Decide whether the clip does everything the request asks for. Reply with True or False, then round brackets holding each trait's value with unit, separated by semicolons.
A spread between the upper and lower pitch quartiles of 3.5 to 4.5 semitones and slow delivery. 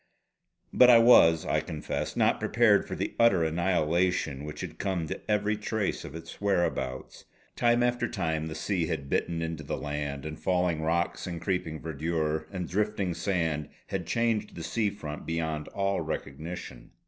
False (4.1 semitones; 165 wpm)